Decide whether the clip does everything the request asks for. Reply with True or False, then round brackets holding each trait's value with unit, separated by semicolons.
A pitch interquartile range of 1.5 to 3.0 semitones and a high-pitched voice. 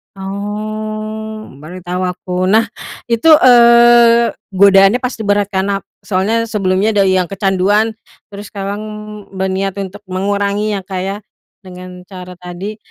True (2.4 semitones; 200 Hz)